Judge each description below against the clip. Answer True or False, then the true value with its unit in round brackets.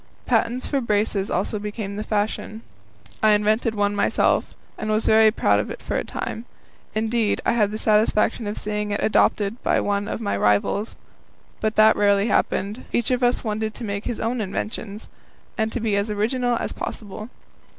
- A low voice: False (215 Hz)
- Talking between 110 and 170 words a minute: False (180 wpm)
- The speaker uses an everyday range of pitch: False (1.5 semitones)